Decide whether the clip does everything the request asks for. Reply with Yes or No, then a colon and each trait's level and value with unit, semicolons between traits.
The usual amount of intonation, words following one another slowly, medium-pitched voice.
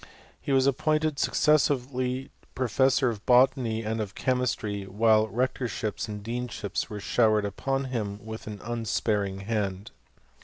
No: average, 3.6 semitones; slow, 130 wpm; low, 115 Hz